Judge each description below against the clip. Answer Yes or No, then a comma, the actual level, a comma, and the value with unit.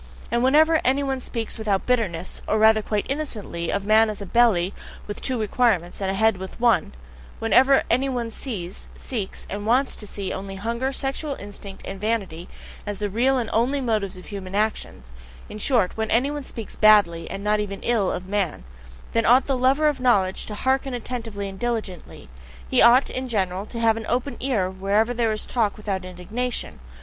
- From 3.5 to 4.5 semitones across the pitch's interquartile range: Yes, average, 4.1 semitones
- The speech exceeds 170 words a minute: Yes, average, 190 wpm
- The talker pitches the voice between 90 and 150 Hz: No, high, 220 Hz